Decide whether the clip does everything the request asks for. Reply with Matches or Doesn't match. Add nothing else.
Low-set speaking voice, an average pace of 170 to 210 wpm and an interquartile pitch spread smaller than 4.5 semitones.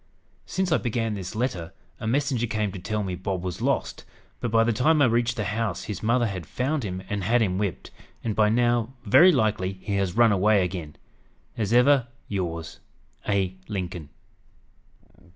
Matches